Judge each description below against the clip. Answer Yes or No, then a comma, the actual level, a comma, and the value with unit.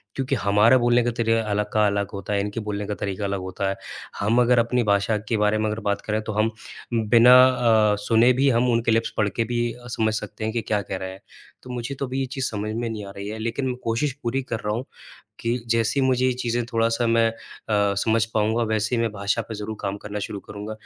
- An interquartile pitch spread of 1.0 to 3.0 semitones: Yes, narrow, 2.4 semitones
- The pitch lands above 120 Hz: No, low, 110 Hz